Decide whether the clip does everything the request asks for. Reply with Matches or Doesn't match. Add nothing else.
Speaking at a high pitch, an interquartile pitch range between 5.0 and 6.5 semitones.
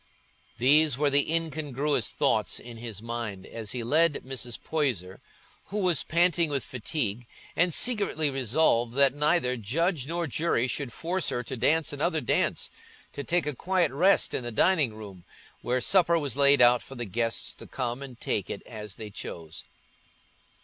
Doesn't match